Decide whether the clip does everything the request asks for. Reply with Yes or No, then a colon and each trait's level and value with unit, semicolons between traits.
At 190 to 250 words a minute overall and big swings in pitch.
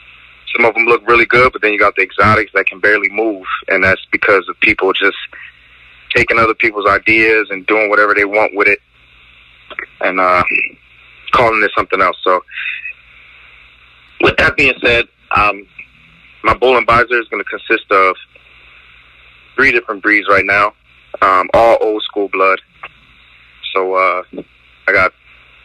No: average, 155 wpm; wide, 9.0 semitones